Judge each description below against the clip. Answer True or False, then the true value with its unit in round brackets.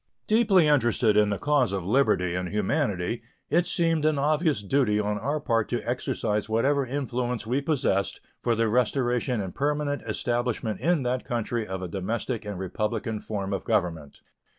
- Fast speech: False (165 wpm)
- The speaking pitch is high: False (120 Hz)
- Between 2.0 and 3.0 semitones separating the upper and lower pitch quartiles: False (5.2 semitones)